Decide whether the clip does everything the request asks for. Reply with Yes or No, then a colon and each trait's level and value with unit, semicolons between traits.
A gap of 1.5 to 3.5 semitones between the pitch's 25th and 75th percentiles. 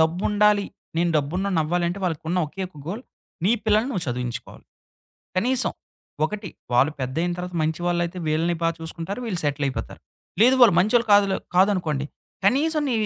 No: average, 4.4 semitones